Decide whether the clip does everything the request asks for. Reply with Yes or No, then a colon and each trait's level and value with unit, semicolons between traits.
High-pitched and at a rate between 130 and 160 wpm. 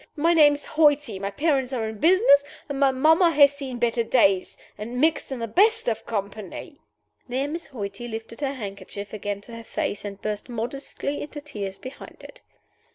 No: very high, 255 Hz; average, 185 wpm